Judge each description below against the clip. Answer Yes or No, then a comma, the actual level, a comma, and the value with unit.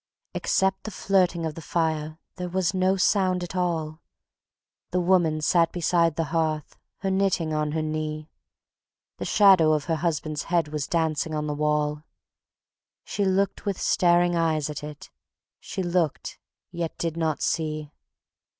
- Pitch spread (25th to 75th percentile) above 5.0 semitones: No, average, 2.8 semitones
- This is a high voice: No, medium, 165 Hz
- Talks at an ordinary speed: Yes, average, 150 wpm